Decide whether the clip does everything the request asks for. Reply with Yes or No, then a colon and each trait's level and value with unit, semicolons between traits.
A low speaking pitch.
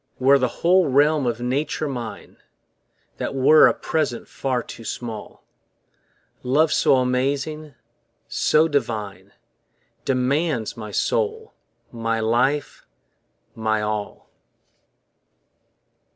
Yes: low, 130 Hz